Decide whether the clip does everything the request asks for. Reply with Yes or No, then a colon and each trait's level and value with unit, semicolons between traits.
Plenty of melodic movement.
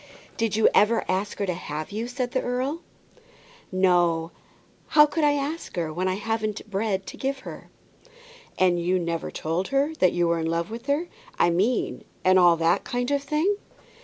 Yes: wide, 6.8 semitones